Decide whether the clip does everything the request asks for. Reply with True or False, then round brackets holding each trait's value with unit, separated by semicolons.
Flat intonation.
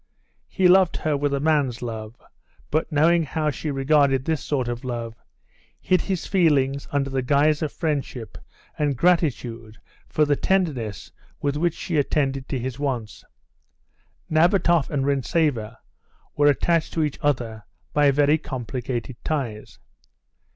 False (3.7 semitones)